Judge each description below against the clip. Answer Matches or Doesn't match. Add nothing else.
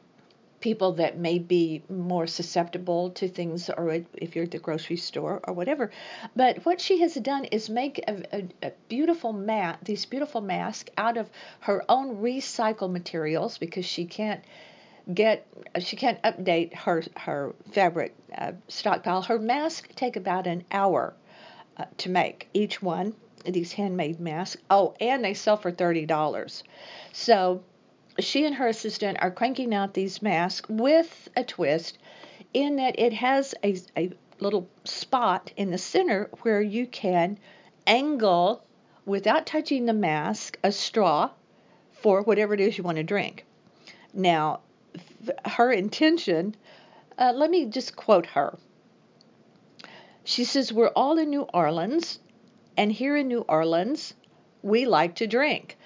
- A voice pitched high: Matches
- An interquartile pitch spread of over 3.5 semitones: Matches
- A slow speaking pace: Doesn't match